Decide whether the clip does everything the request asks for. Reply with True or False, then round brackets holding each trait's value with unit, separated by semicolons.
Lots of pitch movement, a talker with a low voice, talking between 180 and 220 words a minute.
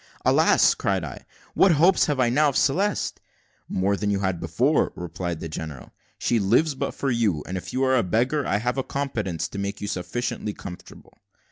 True (6.6 semitones; 115 Hz; 200 wpm)